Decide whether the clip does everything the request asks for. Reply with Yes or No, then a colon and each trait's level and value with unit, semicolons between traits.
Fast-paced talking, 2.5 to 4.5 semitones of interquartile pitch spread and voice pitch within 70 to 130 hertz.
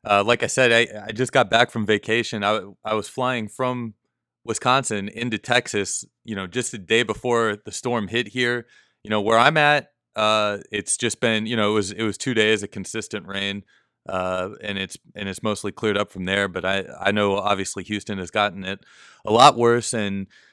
Yes: fast, 210 wpm; average, 2.8 semitones; low, 105 Hz